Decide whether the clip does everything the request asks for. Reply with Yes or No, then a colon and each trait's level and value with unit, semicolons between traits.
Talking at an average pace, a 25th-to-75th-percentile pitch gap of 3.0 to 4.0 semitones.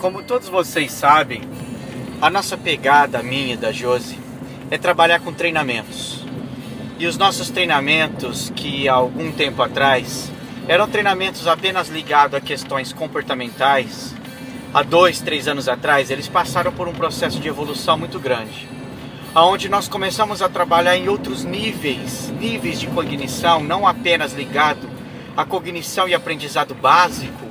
No: average, 140 wpm; average, 5.3 semitones